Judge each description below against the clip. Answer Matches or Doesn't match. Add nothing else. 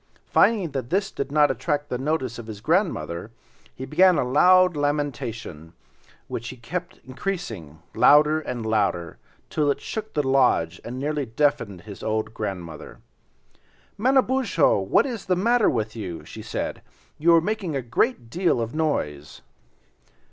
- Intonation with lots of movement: Matches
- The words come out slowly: Doesn't match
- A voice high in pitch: Doesn't match